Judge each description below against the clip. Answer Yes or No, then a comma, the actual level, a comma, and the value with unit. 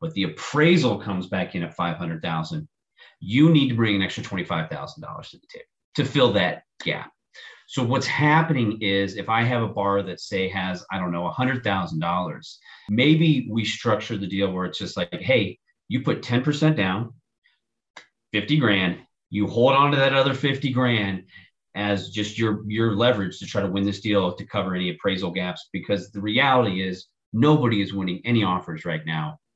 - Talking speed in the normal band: Yes, average, 180 wpm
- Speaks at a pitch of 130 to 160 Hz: No, low, 110 Hz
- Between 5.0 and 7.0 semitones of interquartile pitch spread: Yes, wide, 5.6 semitones